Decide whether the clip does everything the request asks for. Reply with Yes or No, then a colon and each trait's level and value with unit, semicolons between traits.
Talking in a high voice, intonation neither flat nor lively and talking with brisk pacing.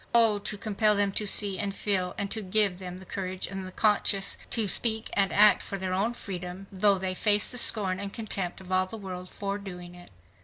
No: high, 195 Hz; narrow, 2.1 semitones; fast, 225 wpm